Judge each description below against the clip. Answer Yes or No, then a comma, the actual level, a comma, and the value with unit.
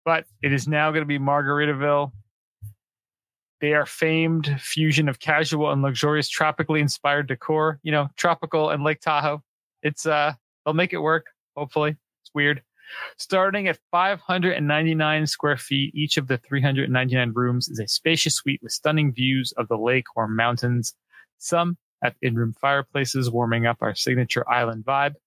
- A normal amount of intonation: Yes, average, 3.2 semitones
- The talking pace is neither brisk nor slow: Yes, average, 155 wpm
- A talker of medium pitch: Yes, medium, 145 Hz